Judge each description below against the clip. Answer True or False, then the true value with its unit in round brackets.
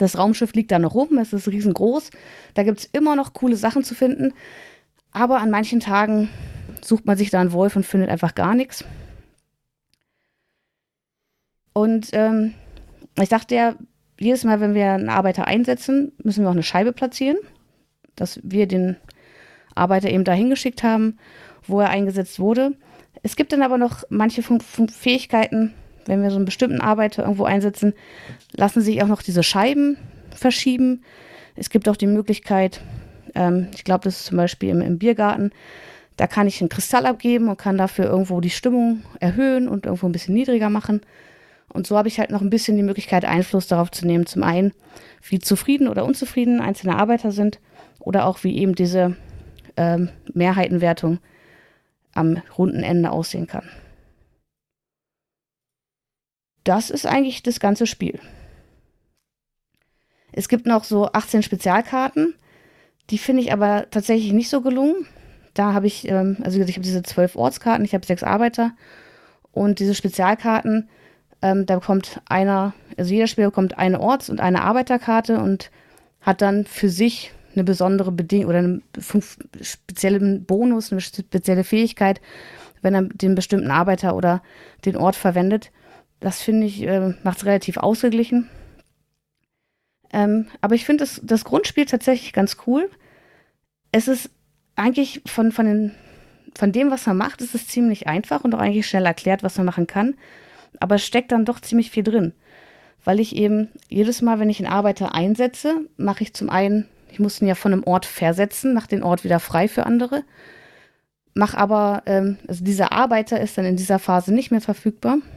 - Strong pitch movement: False (3.7 semitones)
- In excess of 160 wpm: True (170 wpm)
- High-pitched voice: True (205 Hz)